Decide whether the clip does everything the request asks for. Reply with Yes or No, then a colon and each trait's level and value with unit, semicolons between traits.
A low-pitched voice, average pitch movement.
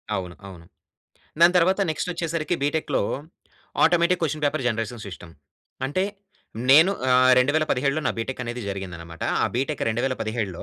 No: low, 130 Hz; wide, 6.3 semitones